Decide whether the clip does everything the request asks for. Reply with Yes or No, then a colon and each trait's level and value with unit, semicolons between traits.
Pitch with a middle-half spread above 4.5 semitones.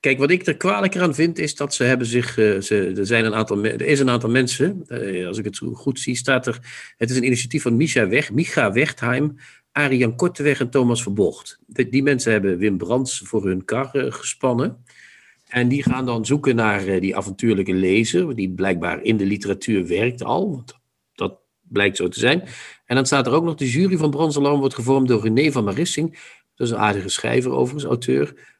Yes: average, 5.0 semitones